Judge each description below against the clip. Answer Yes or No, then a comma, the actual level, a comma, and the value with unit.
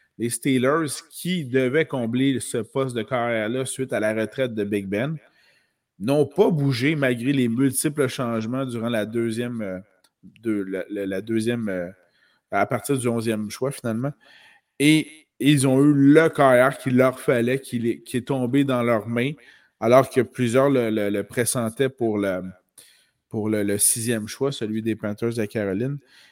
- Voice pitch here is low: Yes, low, 125 Hz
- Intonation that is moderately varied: Yes, average, 3.6 semitones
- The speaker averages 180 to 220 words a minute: No, average, 155 wpm